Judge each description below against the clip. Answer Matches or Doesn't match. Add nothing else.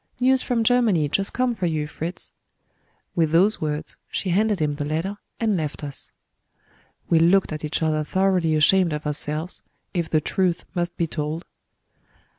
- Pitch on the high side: Doesn't match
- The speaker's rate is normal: Matches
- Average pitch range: Matches